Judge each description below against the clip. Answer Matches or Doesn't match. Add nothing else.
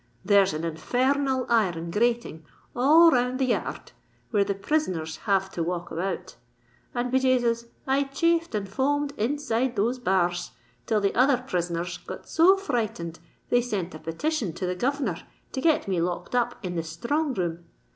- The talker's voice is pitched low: Doesn't match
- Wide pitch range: Matches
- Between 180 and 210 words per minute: Matches